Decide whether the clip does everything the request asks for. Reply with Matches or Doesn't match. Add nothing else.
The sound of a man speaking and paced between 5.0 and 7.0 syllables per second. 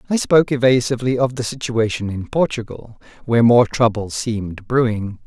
Matches